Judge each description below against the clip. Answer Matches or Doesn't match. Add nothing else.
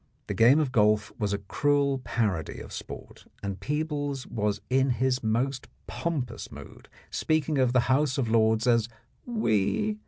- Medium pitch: Doesn't match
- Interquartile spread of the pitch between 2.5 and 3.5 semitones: Doesn't match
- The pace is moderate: Matches